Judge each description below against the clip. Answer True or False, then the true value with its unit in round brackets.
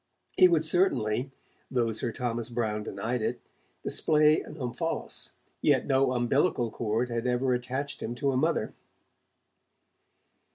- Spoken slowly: True (130 wpm)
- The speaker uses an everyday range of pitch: True (3.3 semitones)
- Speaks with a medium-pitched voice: False (125 Hz)